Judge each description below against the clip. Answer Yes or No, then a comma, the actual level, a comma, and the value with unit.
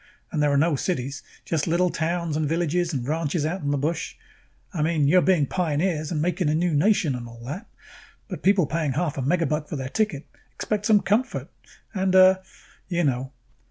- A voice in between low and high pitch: Yes, medium, 160 Hz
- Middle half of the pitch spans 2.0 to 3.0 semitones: No, average, 3.8 semitones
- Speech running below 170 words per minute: No, average, 200 wpm